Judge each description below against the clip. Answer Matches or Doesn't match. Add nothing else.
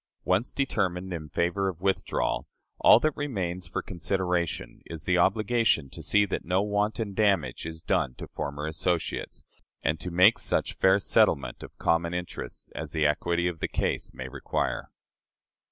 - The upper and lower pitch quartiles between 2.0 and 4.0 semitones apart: Matches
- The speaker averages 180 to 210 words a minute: Doesn't match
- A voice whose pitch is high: Doesn't match